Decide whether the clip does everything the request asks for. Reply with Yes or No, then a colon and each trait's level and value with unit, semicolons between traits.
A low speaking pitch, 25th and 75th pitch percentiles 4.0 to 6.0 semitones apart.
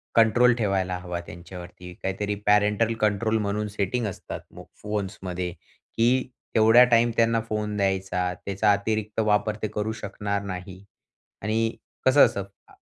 No: low, 105 Hz; narrow, 2.6 semitones